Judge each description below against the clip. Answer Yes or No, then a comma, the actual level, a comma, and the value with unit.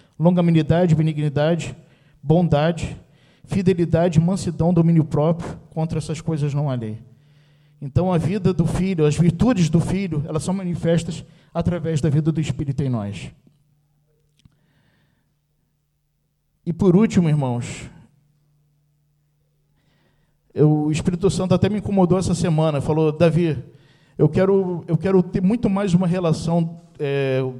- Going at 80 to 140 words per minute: Yes, average, 125 wpm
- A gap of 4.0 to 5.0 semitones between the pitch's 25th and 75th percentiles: No, average, 2.7 semitones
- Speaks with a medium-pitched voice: Yes, medium, 155 Hz